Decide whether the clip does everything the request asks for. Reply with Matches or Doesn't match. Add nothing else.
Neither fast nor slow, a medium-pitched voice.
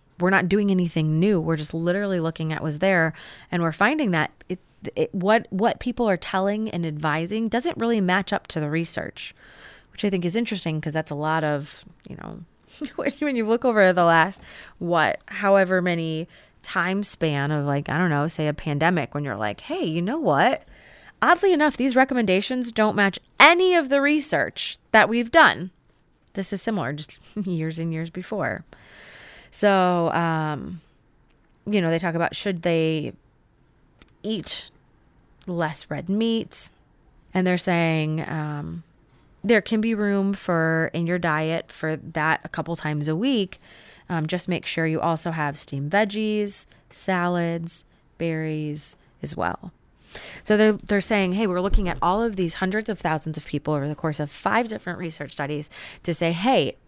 Matches